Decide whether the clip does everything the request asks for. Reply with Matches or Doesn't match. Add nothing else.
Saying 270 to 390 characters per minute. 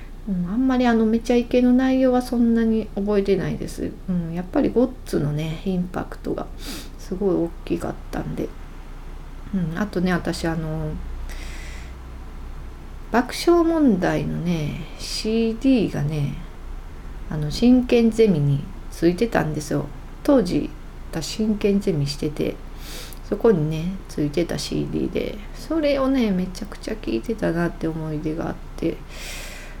Doesn't match